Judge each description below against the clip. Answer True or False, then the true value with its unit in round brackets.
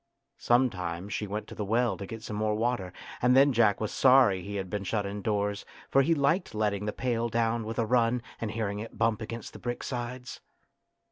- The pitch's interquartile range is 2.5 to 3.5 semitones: True (2.9 semitones)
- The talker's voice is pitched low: True (110 Hz)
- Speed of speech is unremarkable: False (215 wpm)